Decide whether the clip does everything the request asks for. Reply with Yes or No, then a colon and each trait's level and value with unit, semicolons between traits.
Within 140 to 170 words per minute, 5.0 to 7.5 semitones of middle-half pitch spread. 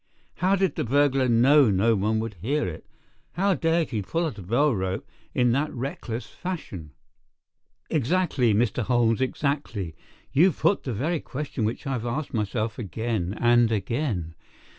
Yes: average, 160 wpm; average, 5.3 semitones